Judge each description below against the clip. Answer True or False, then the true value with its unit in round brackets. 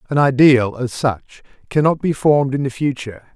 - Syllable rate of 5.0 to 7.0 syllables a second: True (5.3 syllables/s)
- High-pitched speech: False (130 Hz)